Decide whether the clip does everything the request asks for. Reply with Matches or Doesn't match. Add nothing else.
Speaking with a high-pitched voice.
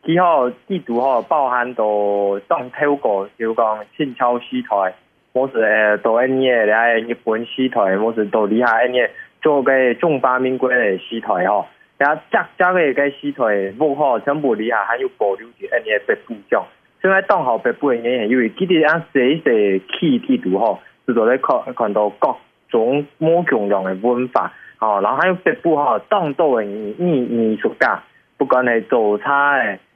Doesn't match